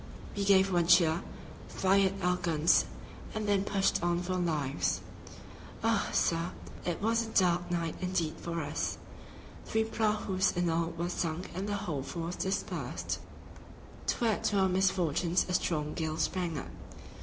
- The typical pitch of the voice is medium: Yes, medium, 175 Hz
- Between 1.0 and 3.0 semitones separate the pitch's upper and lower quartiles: Yes, narrow, 2.6 semitones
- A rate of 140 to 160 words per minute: Yes, average, 155 wpm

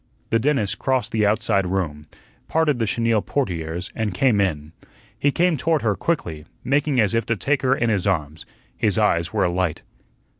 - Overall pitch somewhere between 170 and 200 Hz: No, low, 110 Hz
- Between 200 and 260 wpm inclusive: No, average, 180 wpm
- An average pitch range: No, wide, 6.9 semitones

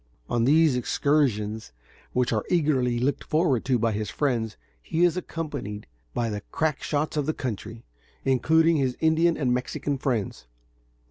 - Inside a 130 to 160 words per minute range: Yes, average, 150 wpm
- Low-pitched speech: Yes, low, 130 Hz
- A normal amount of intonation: Yes, average, 5.0 semitones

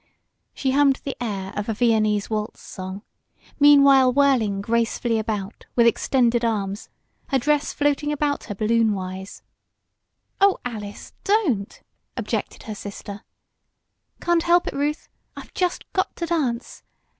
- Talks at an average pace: No, slow, 130 wpm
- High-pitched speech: Yes, high, 235 Hz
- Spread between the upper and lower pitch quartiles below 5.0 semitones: No, wide, 5.5 semitones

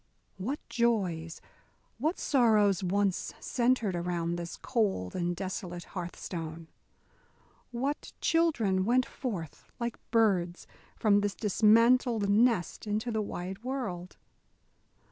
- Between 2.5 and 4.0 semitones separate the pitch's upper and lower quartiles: No, average, 5.0 semitones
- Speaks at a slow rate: Yes, slow, 105 wpm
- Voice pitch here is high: Yes, high, 205 Hz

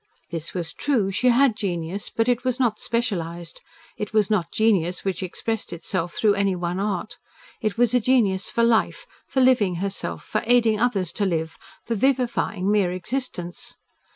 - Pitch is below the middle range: No, high, 205 Hz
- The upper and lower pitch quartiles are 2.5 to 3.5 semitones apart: No, average, 4.8 semitones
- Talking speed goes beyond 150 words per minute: Yes, average, 170 wpm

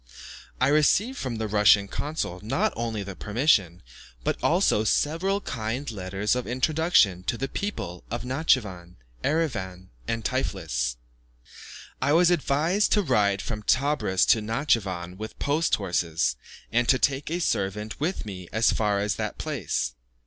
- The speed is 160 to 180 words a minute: No, average, 140 wpm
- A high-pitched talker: No, low, 115 Hz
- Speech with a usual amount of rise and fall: No, wide, 6.9 semitones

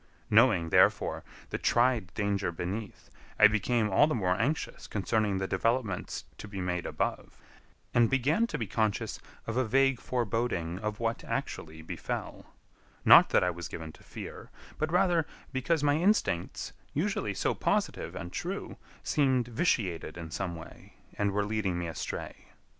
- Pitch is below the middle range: Yes, low, 110 Hz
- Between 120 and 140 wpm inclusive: No, average, 155 wpm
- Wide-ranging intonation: Yes, wide, 6.0 semitones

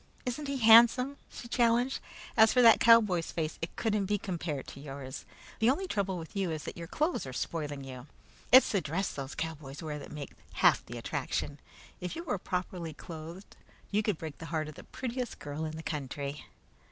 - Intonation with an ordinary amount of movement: No, wide, 7.0 semitones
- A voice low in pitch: No, medium, 175 Hz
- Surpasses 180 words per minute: Yes, average, 200 wpm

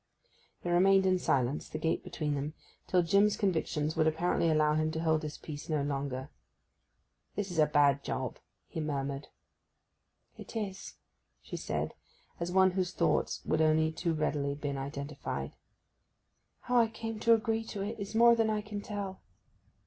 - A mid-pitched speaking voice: Yes, medium, 160 Hz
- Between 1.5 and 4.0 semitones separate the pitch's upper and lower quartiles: No, average, 5.0 semitones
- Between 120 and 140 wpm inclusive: No, average, 165 wpm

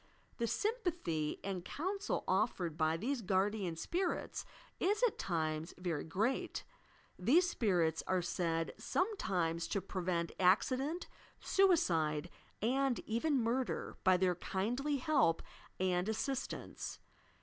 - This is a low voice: No, high, 195 Hz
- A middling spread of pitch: No, wide, 8.2 semitones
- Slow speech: Yes, slow, 110 wpm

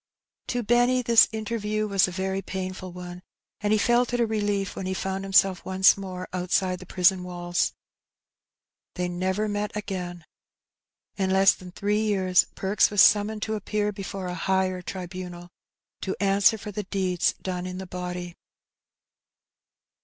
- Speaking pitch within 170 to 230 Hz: Yes, high, 190 Hz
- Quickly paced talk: No, average, 155 wpm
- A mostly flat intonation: Yes, narrow, 2.3 semitones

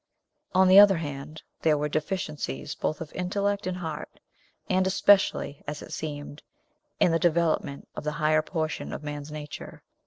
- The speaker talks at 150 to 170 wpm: Yes, average, 160 wpm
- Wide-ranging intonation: No, average, 3.6 semitones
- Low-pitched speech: No, medium, 155 Hz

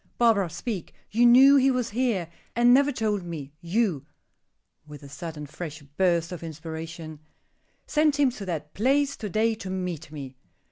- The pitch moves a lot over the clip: Yes, wide, 7.0 semitones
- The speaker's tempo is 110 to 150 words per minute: No, average, 160 wpm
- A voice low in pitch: No, medium, 185 Hz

